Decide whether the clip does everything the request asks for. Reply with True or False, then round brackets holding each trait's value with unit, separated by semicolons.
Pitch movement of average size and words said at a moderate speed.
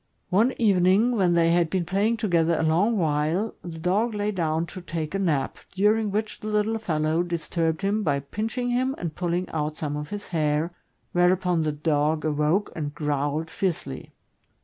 True (4.7 semitones; 175 wpm)